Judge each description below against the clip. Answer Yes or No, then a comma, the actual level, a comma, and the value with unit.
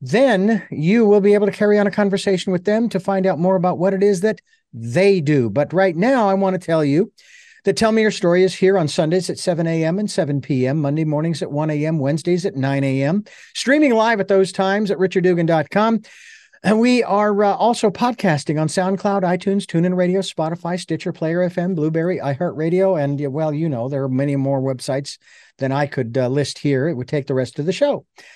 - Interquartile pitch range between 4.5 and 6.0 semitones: Yes, average, 4.9 semitones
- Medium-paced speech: No, fast, 215 wpm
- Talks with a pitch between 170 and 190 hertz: Yes, medium, 185 Hz